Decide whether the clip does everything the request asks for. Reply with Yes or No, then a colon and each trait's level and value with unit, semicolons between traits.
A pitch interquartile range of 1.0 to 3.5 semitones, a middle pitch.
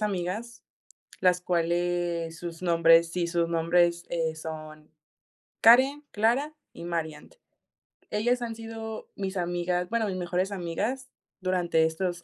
No: average, 4.1 semitones; medium, 175 Hz